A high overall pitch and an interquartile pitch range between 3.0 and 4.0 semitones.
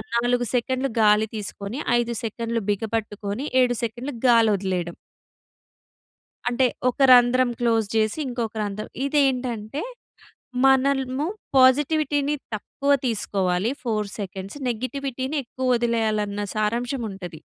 Yes: high, 235 Hz; average, 3.5 semitones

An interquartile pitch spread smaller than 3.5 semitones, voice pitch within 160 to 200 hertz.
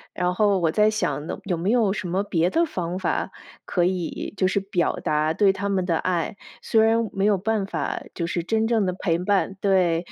Yes: average, 3.0 semitones; high, 190 Hz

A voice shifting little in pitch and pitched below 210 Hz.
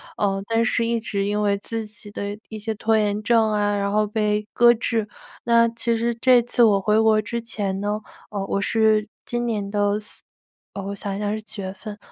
No: narrow, 1.9 semitones; high, 215 Hz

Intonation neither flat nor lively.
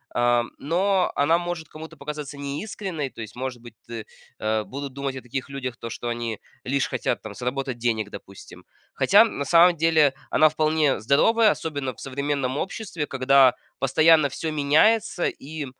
Yes: average, 4.0 semitones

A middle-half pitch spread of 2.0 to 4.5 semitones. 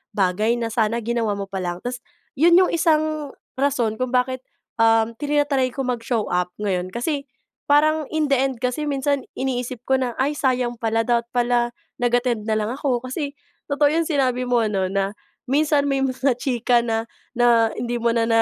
Yes: average, 3.6 semitones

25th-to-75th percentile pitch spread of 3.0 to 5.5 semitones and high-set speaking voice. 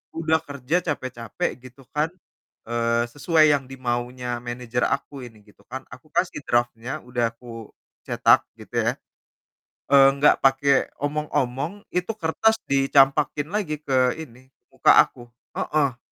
No: average, 3.5 semitones; low, 135 Hz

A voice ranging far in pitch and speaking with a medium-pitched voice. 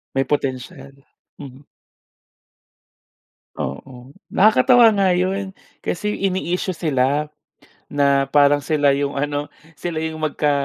No: average, 4.6 semitones; medium, 145 Hz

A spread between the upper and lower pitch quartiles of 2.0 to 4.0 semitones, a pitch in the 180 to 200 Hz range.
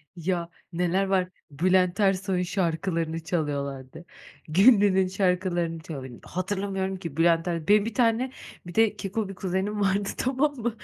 Yes: average, 3.1 semitones; medium, 185 Hz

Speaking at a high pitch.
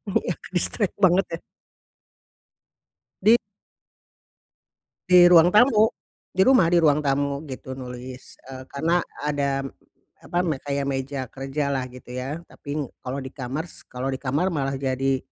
No: medium, 140 Hz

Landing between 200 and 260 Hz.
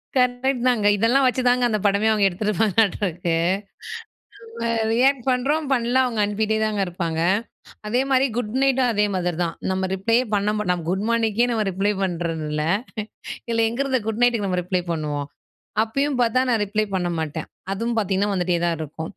Yes: high, 215 Hz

